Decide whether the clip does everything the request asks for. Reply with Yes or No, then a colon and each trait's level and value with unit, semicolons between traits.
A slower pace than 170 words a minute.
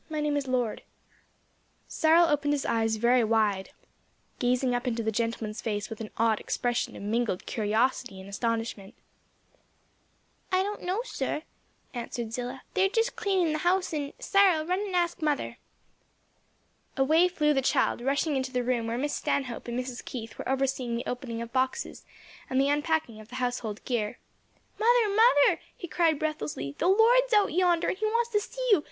No: average, 175 wpm